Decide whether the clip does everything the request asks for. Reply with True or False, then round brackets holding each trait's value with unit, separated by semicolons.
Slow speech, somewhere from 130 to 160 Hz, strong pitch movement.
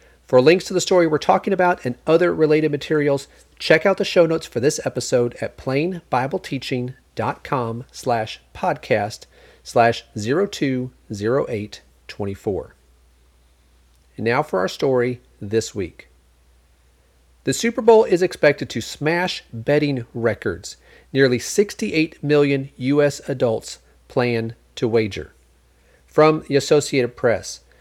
True (115 wpm; 135 Hz; 6.5 semitones)